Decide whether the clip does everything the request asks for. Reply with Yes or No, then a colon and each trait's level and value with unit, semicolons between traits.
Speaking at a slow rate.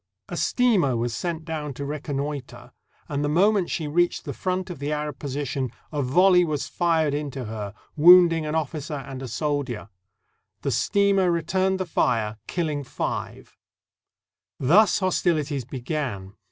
No: average, 145 wpm